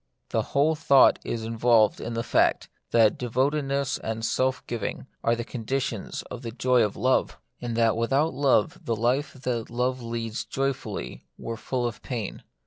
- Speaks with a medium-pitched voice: No, low, 120 Hz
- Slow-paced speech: No, average, 170 wpm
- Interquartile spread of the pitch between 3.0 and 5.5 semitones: No, narrow, 2.4 semitones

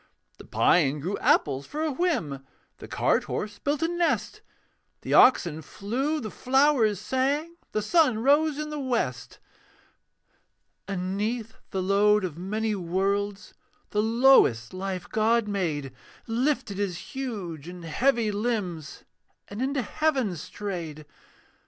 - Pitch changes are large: Yes, wide, 6.4 semitones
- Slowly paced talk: Yes, slow, 130 wpm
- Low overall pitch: No, high, 210 Hz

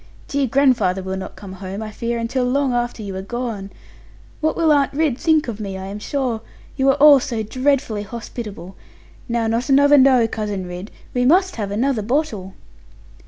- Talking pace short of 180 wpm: No, average, 185 wpm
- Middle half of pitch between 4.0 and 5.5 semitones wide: Yes, average, 5.1 semitones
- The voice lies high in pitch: Yes, high, 235 Hz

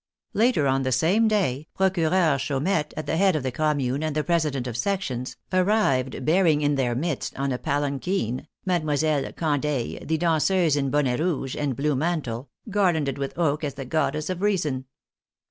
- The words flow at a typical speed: Yes, average, 175 wpm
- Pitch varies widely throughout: No, average, 4.2 semitones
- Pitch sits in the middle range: Yes, medium, 150 Hz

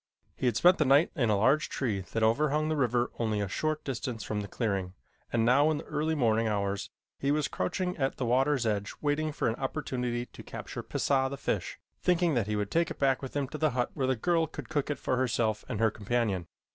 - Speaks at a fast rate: Yes, fast, 235 wpm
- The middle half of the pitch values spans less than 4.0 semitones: No, average, 5.0 semitones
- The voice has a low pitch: Yes, low, 130 Hz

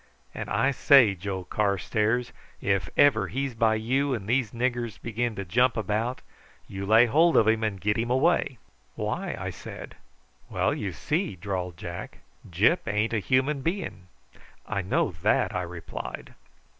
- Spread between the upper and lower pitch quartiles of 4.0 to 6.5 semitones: Yes, average, 4.6 semitones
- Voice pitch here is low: Yes, low, 110 Hz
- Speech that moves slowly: No, average, 155 wpm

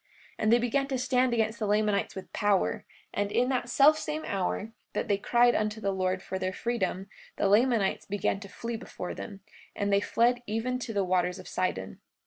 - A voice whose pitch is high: Yes, high, 215 Hz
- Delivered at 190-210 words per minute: Yes, average, 200 wpm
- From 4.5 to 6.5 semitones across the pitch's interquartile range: No, average, 3.7 semitones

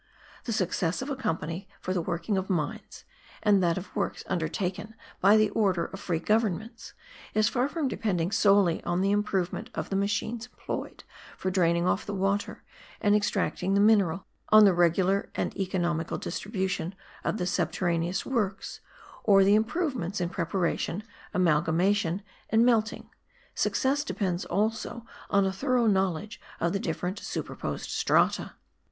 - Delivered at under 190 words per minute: Yes, average, 150 wpm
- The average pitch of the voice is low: No, high, 195 Hz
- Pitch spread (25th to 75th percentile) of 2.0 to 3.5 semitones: Yes, average, 3.2 semitones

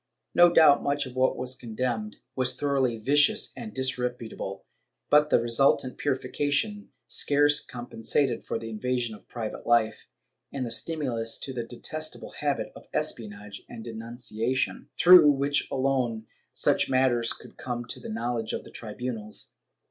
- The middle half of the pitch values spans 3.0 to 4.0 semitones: Yes, average, 3.7 semitones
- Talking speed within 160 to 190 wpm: No, average, 150 wpm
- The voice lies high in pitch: No, low, 125 Hz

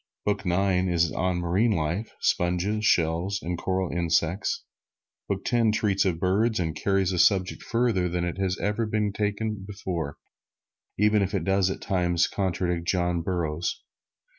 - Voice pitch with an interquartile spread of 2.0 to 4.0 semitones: Yes, average, 2.8 semitones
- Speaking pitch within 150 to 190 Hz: No, very low, 95 Hz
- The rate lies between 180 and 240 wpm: No, average, 155 wpm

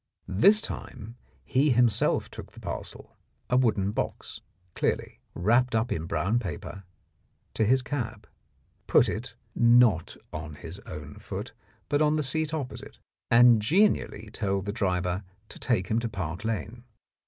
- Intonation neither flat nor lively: Yes, average, 4.4 semitones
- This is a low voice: Yes, low, 110 Hz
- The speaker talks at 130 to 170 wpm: Yes, average, 145 wpm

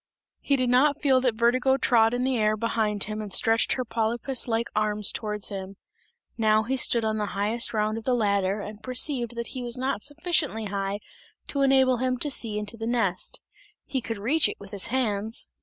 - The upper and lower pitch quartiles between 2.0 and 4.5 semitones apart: Yes, average, 3.3 semitones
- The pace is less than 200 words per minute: No, fast, 205 wpm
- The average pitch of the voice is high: Yes, high, 230 Hz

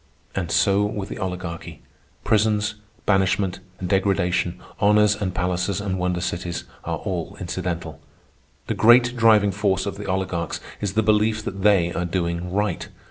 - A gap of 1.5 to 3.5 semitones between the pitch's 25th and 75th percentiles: Yes, narrow, 2.6 semitones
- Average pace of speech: Yes, average, 150 wpm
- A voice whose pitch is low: Yes, very low, 95 Hz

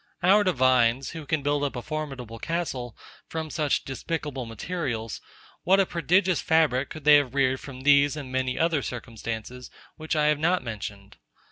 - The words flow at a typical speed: Yes, average, 165 wpm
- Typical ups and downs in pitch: Yes, average, 4.2 semitones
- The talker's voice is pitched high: No, medium, 140 Hz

